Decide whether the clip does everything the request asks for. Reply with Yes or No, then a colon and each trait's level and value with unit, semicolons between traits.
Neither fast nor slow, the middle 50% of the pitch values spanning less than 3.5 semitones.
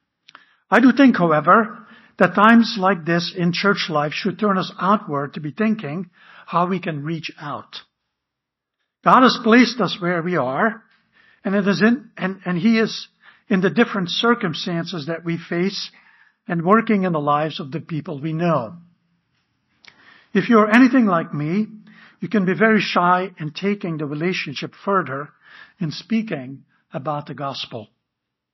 No: average, 160 wpm; average, 4.5 semitones